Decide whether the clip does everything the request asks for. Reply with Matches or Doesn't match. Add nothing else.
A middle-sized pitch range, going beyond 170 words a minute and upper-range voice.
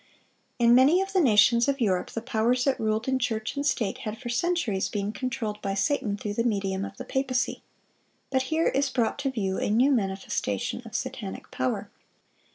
Matches